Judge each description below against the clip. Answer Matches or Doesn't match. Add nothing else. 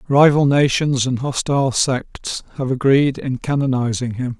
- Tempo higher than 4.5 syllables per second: Doesn't match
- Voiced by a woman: Doesn't match